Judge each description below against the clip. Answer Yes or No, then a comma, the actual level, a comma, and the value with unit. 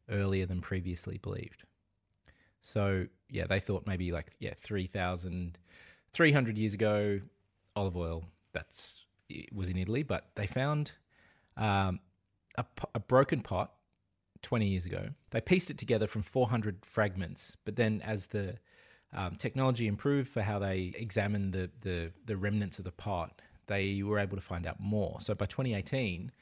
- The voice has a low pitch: Yes, low, 100 Hz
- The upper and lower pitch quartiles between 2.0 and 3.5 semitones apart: Yes, average, 2.9 semitones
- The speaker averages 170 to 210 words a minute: No, average, 155 wpm